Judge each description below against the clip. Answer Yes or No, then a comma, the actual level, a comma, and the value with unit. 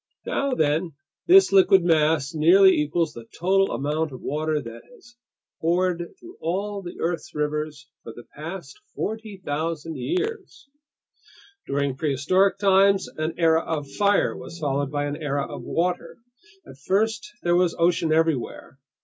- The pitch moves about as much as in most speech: Yes, average, 4.4 semitones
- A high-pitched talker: No, medium, 165 Hz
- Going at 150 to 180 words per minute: No, average, 140 wpm